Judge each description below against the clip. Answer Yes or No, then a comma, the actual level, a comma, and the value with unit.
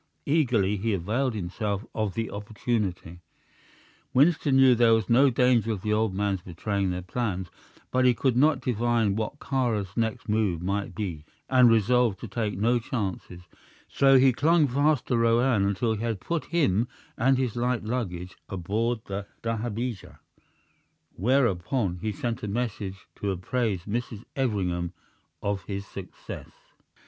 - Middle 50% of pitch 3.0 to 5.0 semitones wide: Yes, average, 4.0 semitones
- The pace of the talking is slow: No, average, 150 wpm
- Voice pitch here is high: No, low, 110 Hz